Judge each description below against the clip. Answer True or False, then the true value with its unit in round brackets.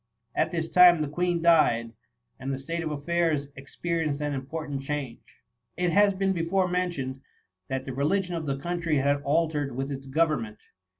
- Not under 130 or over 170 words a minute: False (185 wpm)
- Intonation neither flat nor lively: True (3.8 semitones)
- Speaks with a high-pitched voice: False (150 Hz)